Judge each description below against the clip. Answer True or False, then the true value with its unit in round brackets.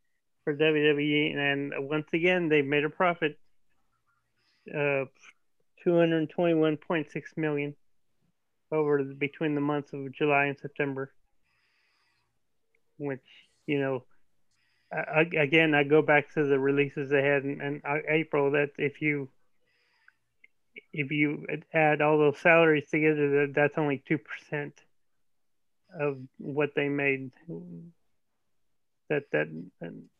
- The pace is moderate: False (120 wpm)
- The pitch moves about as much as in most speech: False (1.5 semitones)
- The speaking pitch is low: False (145 Hz)